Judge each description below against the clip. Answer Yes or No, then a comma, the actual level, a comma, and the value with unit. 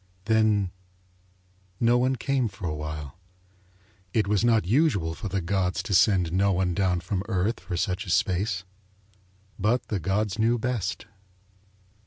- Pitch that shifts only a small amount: No, average, 3.6 semitones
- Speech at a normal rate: Yes, average, 150 wpm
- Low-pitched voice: Yes, low, 100 Hz